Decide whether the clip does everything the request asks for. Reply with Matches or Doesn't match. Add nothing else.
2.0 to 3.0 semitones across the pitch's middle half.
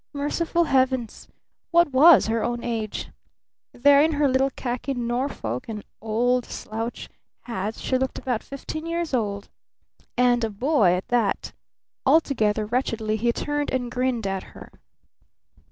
Doesn't match